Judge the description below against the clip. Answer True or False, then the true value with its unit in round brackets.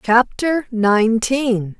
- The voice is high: True (235 Hz)